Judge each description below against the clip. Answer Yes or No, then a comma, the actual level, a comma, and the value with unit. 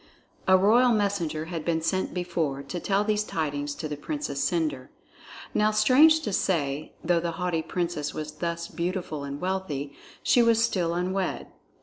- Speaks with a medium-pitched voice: Yes, medium, 175 Hz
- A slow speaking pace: No, average, 160 wpm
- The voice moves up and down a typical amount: Yes, average, 4.4 semitones